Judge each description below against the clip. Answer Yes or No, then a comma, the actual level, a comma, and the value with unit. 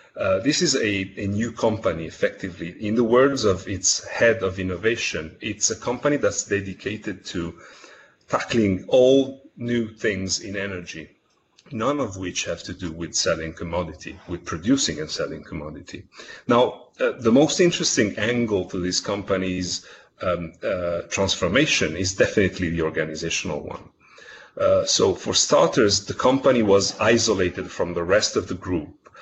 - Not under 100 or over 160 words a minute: Yes, average, 150 wpm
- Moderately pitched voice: No, low, 100 Hz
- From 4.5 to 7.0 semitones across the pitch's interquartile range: Yes, average, 4.8 semitones